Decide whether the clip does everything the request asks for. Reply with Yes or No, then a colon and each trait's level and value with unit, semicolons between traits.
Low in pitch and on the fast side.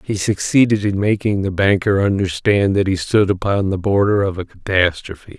No: low, 100 Hz; average, 180 wpm